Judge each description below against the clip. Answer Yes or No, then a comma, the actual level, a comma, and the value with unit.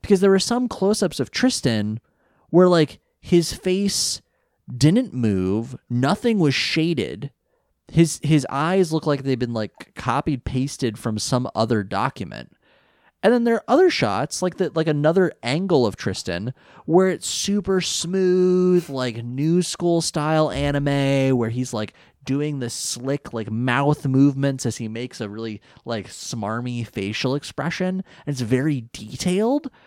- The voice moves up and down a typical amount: No, wide, 7.0 semitones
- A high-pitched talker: No, medium, 140 Hz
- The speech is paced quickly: No, average, 150 wpm